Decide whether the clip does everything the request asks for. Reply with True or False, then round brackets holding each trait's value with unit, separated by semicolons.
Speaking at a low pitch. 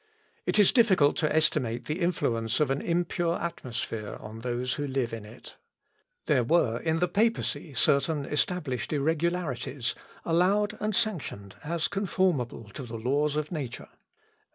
False (150 Hz)